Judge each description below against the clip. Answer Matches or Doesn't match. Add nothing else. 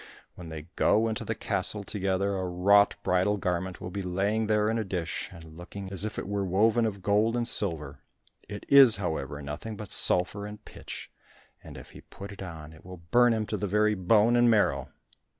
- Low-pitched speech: Matches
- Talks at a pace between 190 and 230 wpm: Matches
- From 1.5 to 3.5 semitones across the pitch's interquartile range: Matches